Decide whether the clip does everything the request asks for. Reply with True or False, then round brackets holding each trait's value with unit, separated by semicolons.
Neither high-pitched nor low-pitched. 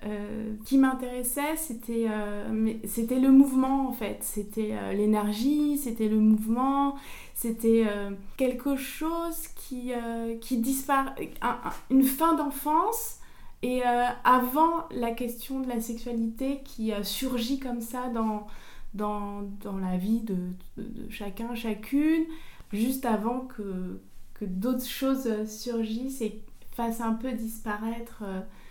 False (235 Hz)